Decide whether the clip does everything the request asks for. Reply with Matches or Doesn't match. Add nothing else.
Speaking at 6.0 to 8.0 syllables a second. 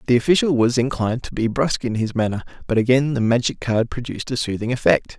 Matches